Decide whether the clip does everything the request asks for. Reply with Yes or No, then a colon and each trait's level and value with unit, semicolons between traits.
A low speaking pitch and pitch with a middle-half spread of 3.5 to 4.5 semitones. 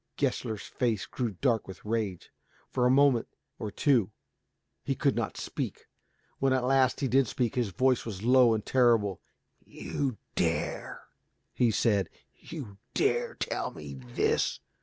Yes: low, 120 Hz; average, 4.0 semitones